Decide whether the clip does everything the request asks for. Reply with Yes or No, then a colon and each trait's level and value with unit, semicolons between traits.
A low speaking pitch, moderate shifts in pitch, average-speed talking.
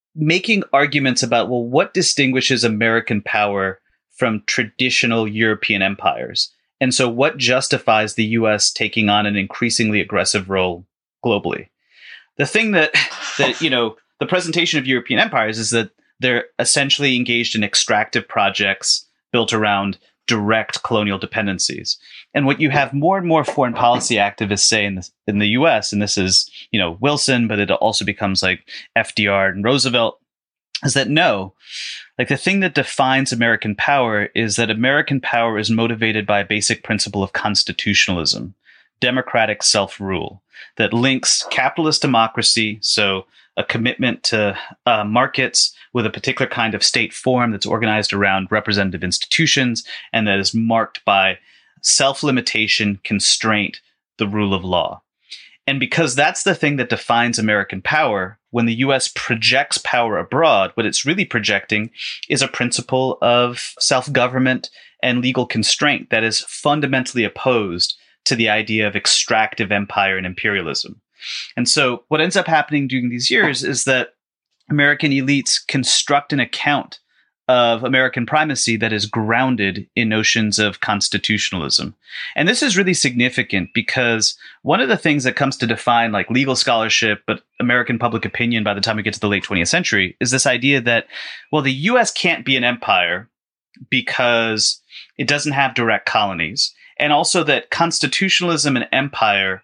Yes: low, 115 Hz; average, 4.2 semitones; average, 155 wpm